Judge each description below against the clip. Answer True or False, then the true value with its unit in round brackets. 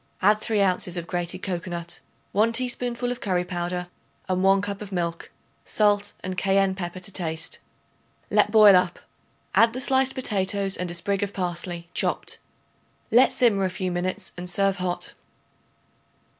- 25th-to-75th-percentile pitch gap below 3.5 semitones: True (2.7 semitones)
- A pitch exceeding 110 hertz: True (190 Hz)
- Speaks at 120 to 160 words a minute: True (155 wpm)